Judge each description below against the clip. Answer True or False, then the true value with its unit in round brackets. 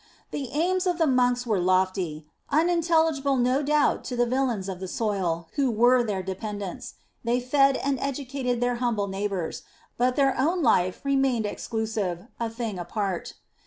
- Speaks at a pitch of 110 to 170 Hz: False (245 Hz)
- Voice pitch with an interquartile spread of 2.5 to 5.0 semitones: False (5.4 semitones)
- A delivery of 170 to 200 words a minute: False (160 wpm)